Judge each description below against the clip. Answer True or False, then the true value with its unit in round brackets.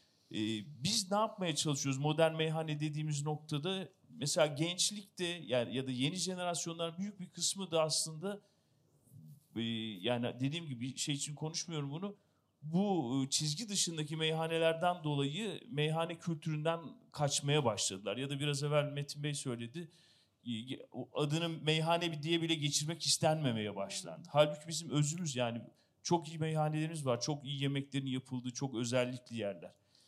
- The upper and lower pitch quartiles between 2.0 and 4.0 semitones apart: True (3.5 semitones)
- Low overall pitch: False (150 Hz)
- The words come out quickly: False (130 wpm)